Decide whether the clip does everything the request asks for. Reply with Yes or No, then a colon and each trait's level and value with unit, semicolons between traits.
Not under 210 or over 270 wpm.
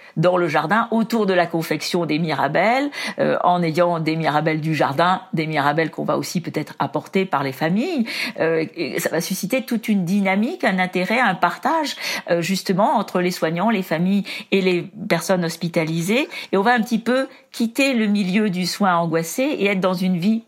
No: average, 195 wpm